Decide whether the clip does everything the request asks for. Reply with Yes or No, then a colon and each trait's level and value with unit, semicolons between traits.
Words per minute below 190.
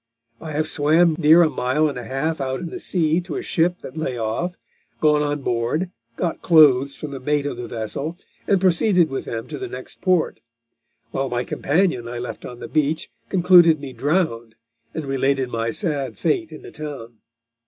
No: average, 195 wpm